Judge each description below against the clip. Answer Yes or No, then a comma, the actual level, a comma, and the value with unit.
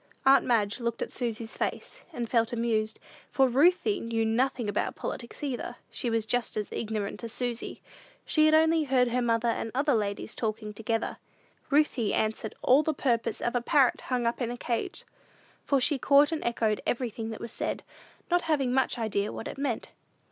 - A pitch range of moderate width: Yes, average, 3.1 semitones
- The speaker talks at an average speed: Yes, average, 185 wpm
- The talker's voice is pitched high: Yes, high, 240 Hz